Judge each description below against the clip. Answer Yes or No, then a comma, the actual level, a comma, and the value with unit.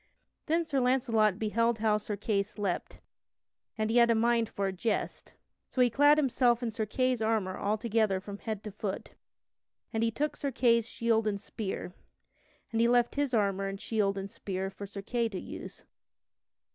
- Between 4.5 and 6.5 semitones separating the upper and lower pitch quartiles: No, average, 2.9 semitones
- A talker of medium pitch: No, high, 220 Hz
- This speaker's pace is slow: No, average, 185 wpm